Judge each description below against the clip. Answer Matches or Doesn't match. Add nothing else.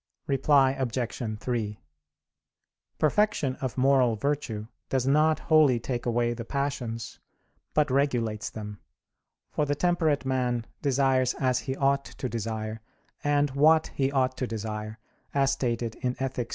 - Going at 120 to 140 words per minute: Matches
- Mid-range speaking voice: Doesn't match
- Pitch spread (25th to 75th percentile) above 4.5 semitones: Doesn't match